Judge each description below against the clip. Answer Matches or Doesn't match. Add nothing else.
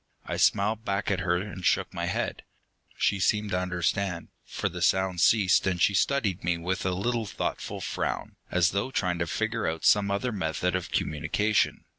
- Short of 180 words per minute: Doesn't match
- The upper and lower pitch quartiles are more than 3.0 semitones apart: Doesn't match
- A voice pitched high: Doesn't match